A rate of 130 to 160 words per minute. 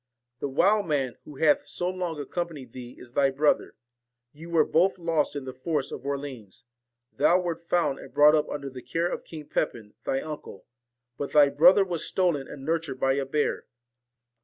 No: average, 185 wpm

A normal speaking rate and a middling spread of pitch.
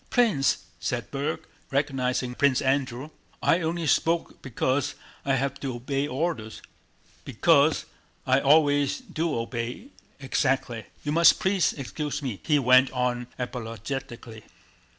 No: slow, 120 wpm; average, 3.2 semitones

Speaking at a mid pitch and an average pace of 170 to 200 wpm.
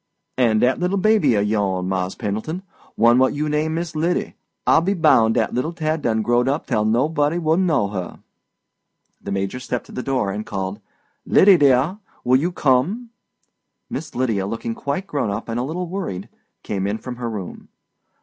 No: low, 125 Hz; average, 180 wpm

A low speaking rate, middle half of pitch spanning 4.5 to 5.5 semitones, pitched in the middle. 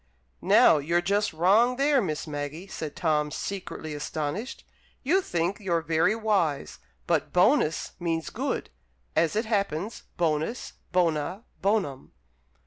Yes: slow, 130 wpm; average, 5.1 semitones; medium, 175 Hz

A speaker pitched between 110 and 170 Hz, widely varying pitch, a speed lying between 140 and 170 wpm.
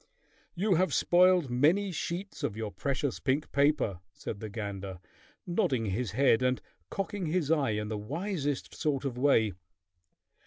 Yes: medium, 140 Hz; wide, 7.5 semitones; average, 150 wpm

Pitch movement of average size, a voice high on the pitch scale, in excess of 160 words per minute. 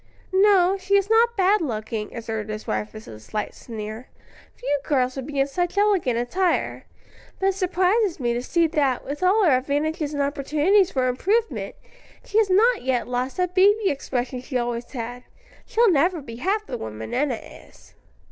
No: wide, 7.7 semitones; very high, 290 Hz; average, 180 wpm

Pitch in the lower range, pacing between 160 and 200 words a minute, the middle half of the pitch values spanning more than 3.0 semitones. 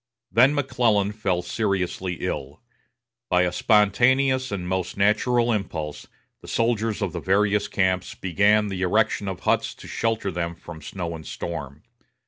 No: low, 100 Hz; average, 145 wpm; average, 3.8 semitones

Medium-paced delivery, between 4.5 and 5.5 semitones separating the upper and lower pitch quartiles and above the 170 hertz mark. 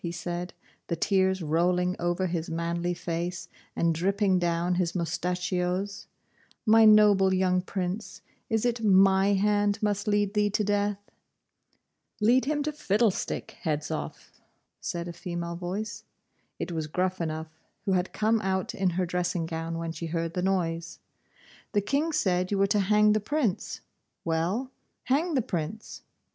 No: average, 150 wpm; average, 3.2 semitones; medium, 185 Hz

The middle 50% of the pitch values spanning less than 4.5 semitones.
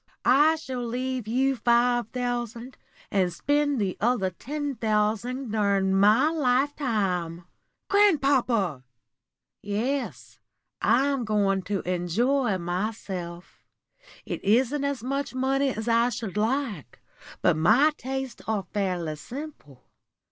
No: average, 5.3 semitones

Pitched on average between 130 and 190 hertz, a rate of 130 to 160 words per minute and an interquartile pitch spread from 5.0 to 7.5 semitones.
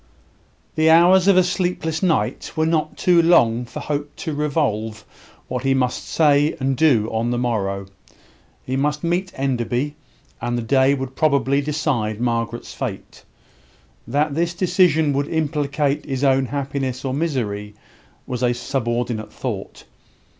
No: medium, 140 Hz; average, 145 wpm; average, 4.4 semitones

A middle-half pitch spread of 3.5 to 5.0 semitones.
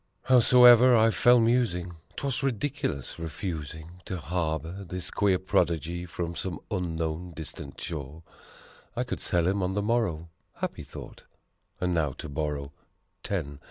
Yes: average, 4.6 semitones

